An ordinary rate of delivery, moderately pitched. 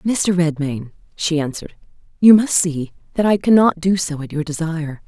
Yes: average, 190 wpm; medium, 170 Hz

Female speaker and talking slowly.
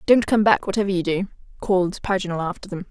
No: female; fast, 205 wpm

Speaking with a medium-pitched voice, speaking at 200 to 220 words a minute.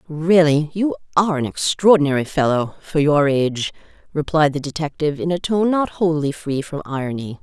No: medium, 155 Hz; average, 145 wpm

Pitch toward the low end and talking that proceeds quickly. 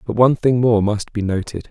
Yes: low, 115 Hz; fast, 245 wpm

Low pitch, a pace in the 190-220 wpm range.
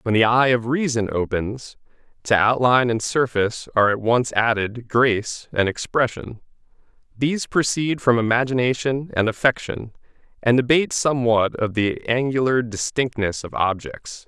No: low, 120 Hz; slow, 135 wpm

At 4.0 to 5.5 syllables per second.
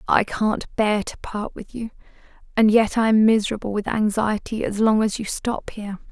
Yes: 5.0 syllables/s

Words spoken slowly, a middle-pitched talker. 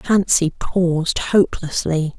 Yes: slow, 80 wpm; medium, 175 Hz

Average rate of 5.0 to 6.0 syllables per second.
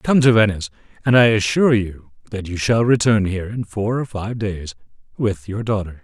Yes: 5.4 syllables/s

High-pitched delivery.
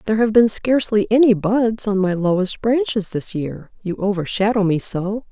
Yes: high, 210 Hz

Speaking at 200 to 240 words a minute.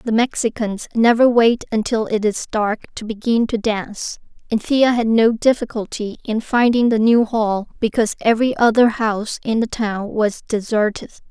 No: average, 165 wpm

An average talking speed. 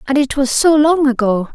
No: fast, 235 wpm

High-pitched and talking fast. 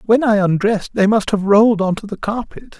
Yes: high, 210 Hz; fast, 235 wpm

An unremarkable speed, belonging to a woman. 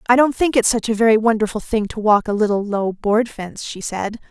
No: fast, 250 wpm; female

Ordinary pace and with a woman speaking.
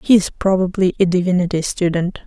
No: slow, 130 wpm; female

